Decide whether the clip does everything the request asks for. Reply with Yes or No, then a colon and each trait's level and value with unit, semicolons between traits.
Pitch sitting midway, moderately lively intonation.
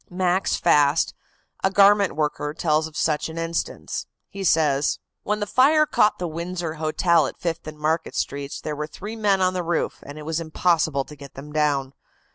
Yes: medium, 160 Hz; average, 3.4 semitones